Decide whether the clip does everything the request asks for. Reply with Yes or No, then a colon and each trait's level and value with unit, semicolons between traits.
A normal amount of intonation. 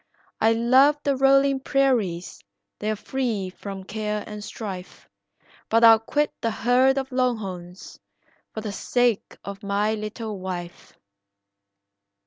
Yes: average, 4.3 semitones